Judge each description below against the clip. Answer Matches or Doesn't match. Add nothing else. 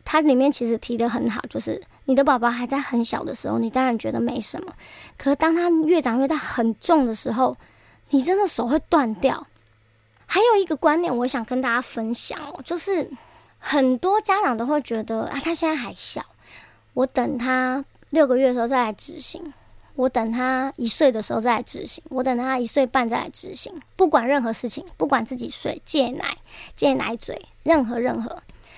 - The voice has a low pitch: Doesn't match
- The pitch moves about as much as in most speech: Matches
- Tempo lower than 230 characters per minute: Doesn't match